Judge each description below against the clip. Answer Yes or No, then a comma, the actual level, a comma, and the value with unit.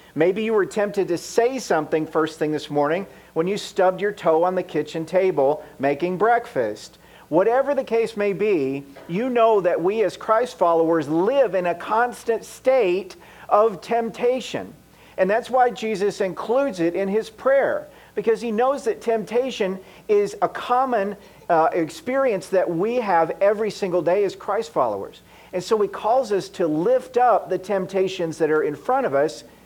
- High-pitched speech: Yes, high, 200 Hz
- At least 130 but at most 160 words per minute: No, average, 170 wpm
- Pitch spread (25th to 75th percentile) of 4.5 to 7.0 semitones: Yes, wide, 5.4 semitones